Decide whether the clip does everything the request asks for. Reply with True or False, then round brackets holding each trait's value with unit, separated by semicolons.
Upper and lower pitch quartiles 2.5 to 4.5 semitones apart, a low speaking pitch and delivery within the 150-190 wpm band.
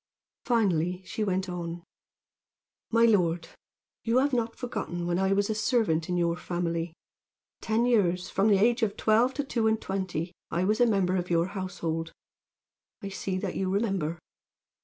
False (4.1 semitones; 190 Hz; 165 wpm)